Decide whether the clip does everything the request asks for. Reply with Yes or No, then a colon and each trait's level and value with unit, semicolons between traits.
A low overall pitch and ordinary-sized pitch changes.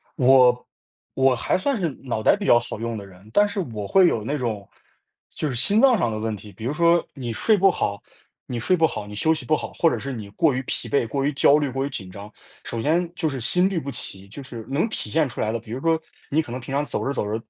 No: low, 130 Hz; wide, 6.2 semitones